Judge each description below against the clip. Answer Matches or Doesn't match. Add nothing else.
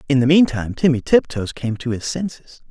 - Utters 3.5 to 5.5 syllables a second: Doesn't match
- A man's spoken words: Matches